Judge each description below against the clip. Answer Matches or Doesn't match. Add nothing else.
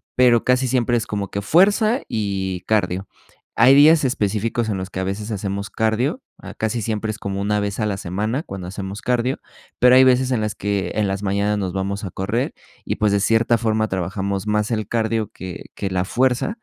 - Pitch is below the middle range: Matches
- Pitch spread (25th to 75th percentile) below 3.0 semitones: Doesn't match